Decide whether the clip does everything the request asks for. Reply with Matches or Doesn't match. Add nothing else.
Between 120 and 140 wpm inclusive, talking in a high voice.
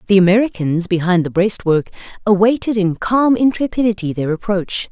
Matches